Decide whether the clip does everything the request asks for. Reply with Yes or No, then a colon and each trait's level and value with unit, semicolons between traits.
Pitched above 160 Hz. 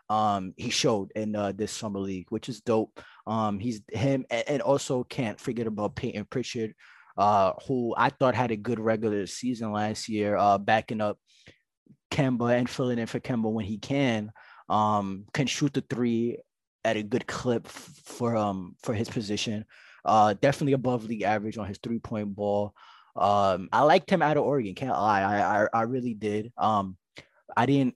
No: low, 115 Hz